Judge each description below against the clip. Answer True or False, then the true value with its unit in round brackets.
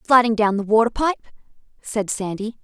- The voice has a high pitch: True (220 Hz)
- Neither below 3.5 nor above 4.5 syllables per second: False (5.3 syllables/s)